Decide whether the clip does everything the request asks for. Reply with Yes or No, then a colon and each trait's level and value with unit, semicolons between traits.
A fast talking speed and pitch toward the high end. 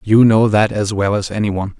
No: fast, 270 wpm; low, 105 Hz